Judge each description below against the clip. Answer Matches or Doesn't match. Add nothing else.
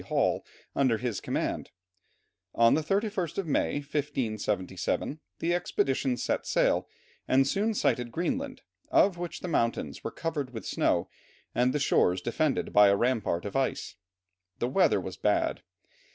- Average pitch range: Doesn't match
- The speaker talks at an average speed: Matches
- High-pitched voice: Doesn't match